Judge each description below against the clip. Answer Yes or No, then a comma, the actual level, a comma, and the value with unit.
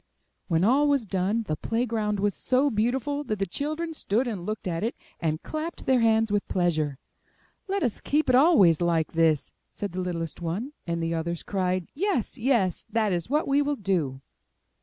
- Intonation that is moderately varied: No, wide, 7.3 semitones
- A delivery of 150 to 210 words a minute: Yes, average, 190 wpm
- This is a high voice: Yes, high, 210 Hz